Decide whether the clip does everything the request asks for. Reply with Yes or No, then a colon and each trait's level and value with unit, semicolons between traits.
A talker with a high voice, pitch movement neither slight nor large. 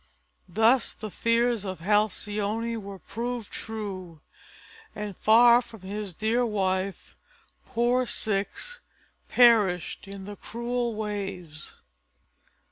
Yes: high, 215 Hz; average, 3.1 semitones